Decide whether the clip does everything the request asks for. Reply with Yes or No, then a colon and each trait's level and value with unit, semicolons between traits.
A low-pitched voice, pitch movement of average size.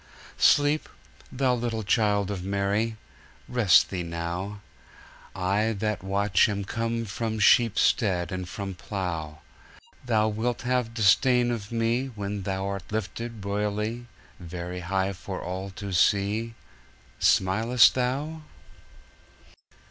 Yes: low, 105 Hz; average, 3.3 semitones